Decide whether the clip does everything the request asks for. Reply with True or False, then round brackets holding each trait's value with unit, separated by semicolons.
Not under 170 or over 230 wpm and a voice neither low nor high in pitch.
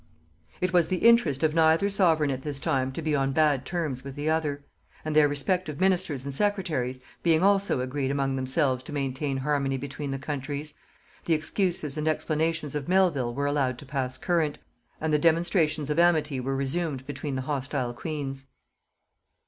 True (175 wpm; 150 Hz)